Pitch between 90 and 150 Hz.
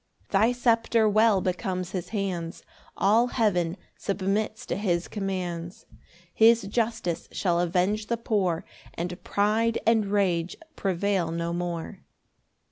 No: high, 195 Hz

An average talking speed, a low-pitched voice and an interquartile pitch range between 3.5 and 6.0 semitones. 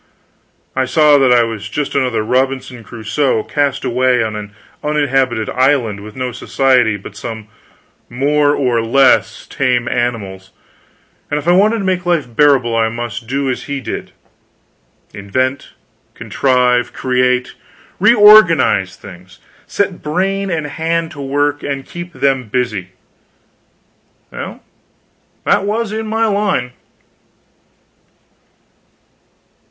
No: slow, 120 wpm; low, 130 Hz; average, 4.2 semitones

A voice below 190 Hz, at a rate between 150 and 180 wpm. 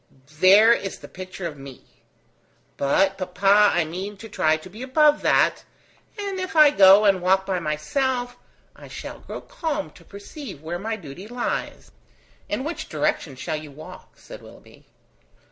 No: high, 195 Hz; average, 165 wpm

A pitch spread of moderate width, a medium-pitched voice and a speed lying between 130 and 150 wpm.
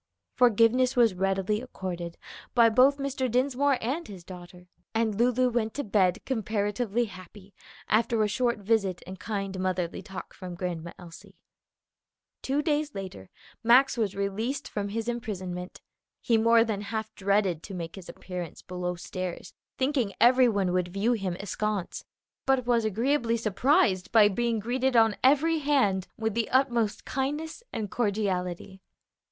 No: average, 4.5 semitones; high, 215 Hz; average, 145 wpm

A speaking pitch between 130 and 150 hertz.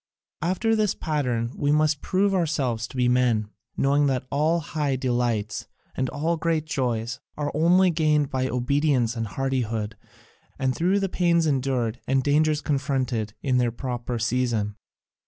Yes: low, 135 Hz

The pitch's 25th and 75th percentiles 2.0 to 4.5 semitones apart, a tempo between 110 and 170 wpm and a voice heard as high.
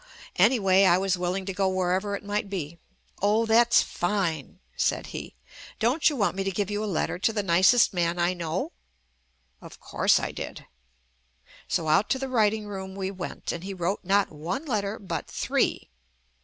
No: average, 2.7 semitones; average, 190 wpm; high, 195 Hz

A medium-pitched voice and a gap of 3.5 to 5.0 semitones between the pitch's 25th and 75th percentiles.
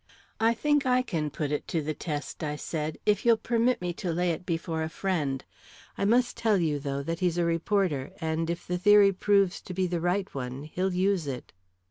Yes: medium, 175 Hz; average, 4.3 semitones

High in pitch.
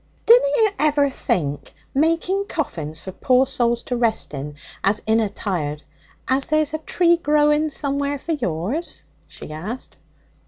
Yes: very high, 270 Hz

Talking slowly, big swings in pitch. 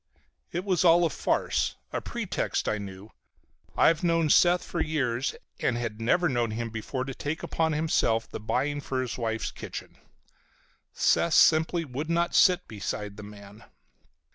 No: average, 160 wpm; wide, 6.6 semitones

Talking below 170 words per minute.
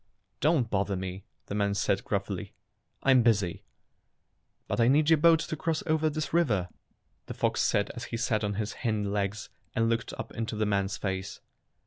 No: average, 180 wpm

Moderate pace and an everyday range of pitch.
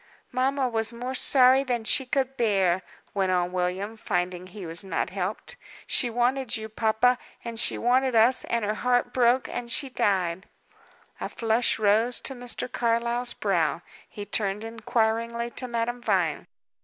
Yes: average, 155 wpm; average, 3.4 semitones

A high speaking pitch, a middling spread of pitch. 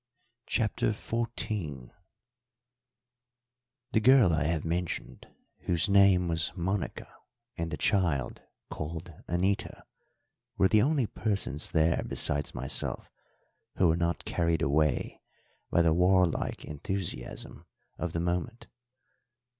No: very low, 85 Hz; average, 3.7 semitones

